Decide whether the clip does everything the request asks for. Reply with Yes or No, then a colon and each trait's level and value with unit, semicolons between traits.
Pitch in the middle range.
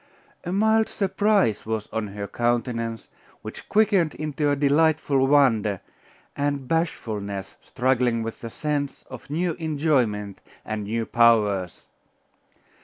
No: low, 130 Hz